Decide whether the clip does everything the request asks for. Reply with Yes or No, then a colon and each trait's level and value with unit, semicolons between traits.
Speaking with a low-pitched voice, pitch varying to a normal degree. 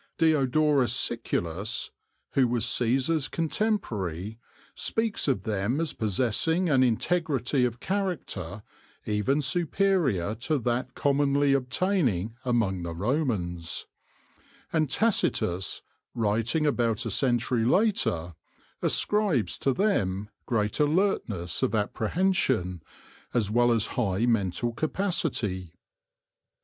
No: low, 120 Hz; wide, 6.8 semitones